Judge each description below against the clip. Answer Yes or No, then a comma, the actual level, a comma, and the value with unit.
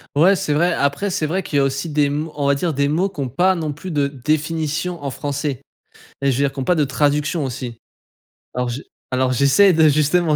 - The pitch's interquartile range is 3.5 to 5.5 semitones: No, average, 2.8 semitones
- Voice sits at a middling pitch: Yes, medium, 145 Hz